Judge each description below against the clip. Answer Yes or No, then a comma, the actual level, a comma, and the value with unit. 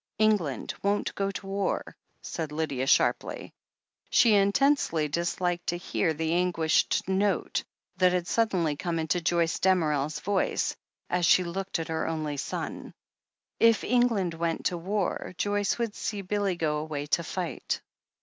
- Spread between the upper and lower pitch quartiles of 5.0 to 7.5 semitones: No, average, 3.7 semitones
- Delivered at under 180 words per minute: Yes, average, 145 wpm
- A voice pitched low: No, medium, 175 Hz